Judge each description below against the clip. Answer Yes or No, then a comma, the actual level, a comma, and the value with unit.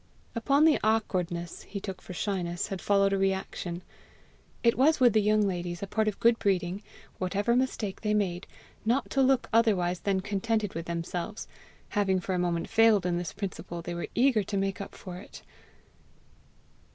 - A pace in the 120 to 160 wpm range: No, average, 175 wpm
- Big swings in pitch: No, average, 3.5 semitones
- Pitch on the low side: No, high, 195 Hz